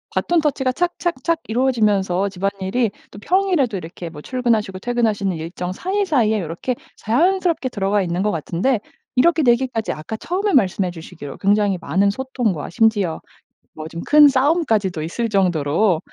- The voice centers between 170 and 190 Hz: No, high, 215 Hz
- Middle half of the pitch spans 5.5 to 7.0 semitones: Yes, wide, 6.1 semitones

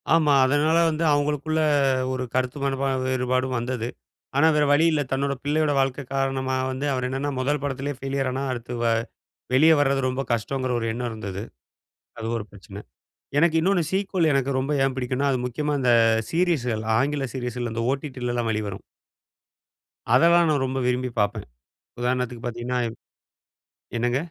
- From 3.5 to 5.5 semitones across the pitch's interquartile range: No, average, 2.8 semitones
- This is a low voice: Yes, low, 130 Hz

